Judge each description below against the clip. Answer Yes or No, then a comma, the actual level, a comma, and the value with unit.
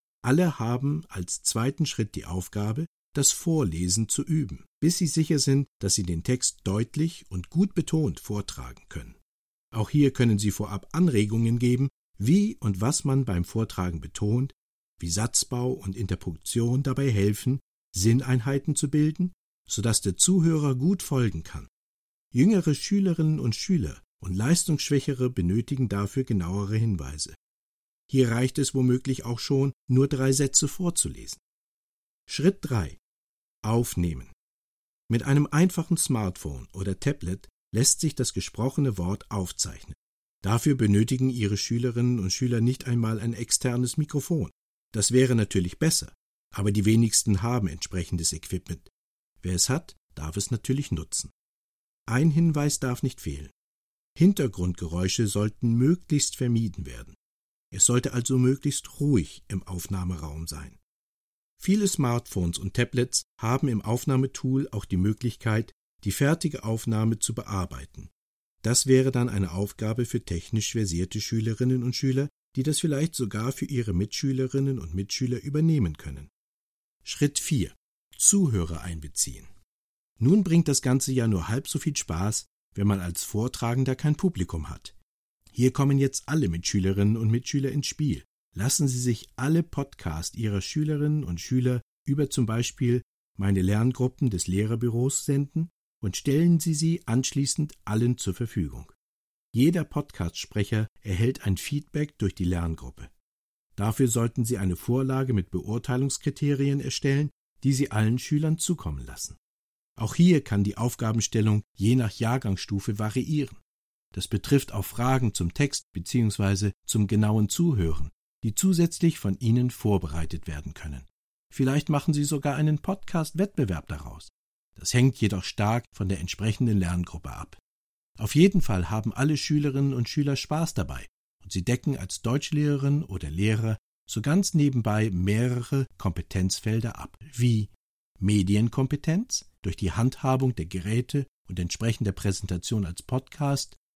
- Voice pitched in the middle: No, low, 120 Hz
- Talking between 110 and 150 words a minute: Yes, average, 135 wpm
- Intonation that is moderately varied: No, wide, 6.2 semitones